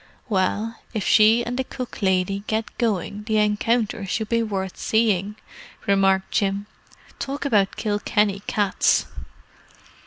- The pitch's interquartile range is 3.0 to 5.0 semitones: No, narrow, 2.5 semitones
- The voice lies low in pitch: No, high, 210 Hz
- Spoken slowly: Yes, slow, 130 wpm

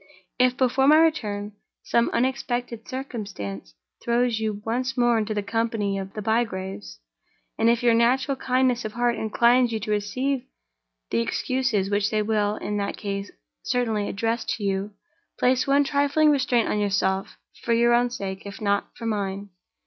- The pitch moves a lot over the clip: No, average, 3.5 semitones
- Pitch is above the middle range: Yes, high, 225 Hz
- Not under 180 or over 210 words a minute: No, average, 165 wpm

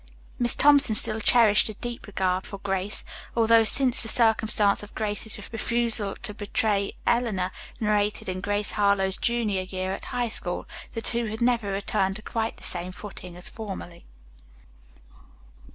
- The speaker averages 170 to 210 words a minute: No, average, 150 wpm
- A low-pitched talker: No, high, 210 Hz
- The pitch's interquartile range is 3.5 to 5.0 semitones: No, average, 2.9 semitones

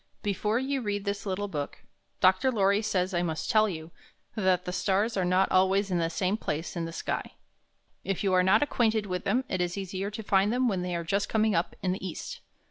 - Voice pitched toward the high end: Yes, high, 195 Hz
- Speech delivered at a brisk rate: Yes, fast, 225 wpm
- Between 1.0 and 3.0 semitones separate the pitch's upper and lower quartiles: Yes, narrow, 2.6 semitones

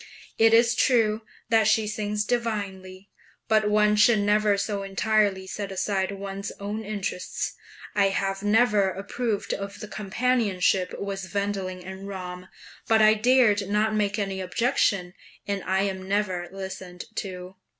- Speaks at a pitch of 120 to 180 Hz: No, high, 200 Hz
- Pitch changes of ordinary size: No, narrow, 1.9 semitones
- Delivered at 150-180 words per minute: No, average, 140 wpm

